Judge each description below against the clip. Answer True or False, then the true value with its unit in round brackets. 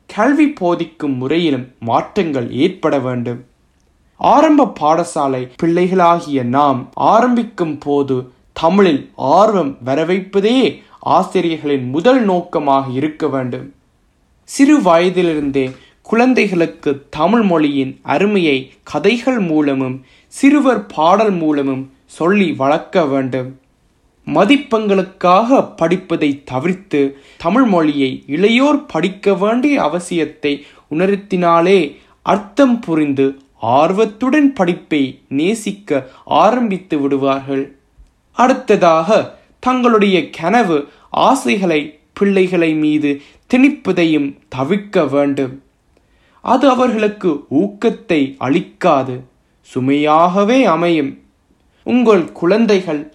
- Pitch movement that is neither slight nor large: False (6.7 semitones)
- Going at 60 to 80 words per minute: True (75 wpm)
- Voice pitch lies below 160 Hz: False (165 Hz)